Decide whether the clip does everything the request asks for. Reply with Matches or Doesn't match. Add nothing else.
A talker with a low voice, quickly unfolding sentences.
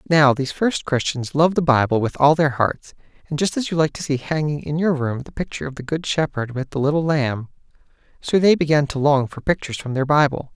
Doesn't match